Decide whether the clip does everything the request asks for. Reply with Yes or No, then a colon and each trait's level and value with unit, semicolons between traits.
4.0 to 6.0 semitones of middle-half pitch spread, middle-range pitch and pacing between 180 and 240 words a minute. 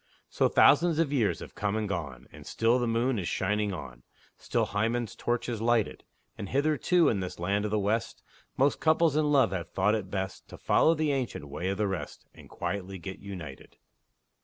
No: average, 5.2 semitones; low, 105 Hz; average, 200 wpm